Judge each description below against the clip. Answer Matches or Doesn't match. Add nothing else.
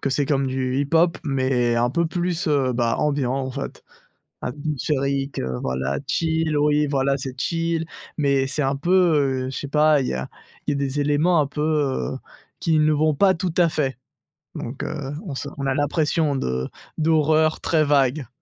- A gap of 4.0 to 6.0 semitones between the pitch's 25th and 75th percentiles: Doesn't match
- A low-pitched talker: Doesn't match